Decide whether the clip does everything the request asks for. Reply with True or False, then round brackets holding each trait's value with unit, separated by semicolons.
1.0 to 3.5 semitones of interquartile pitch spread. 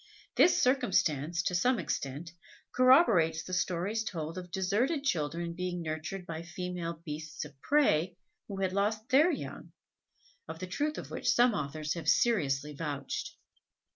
False (5.5 semitones)